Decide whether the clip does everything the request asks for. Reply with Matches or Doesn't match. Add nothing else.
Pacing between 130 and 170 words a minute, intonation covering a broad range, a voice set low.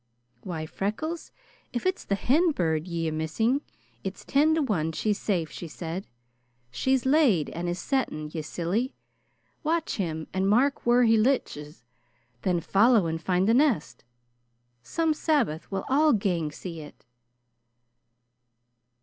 Doesn't match